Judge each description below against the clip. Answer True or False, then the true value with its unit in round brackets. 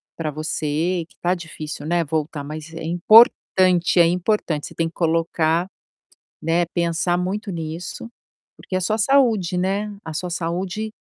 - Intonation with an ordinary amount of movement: False (2.3 semitones)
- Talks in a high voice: False (170 Hz)